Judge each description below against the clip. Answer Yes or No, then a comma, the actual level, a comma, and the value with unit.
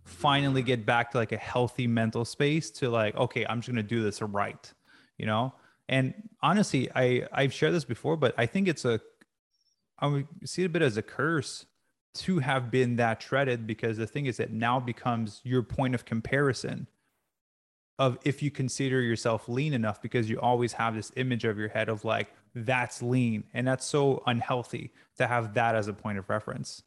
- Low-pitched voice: Yes, low, 120 Hz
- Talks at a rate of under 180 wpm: No, average, 200 wpm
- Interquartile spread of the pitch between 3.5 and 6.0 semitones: No, average, 2.8 semitones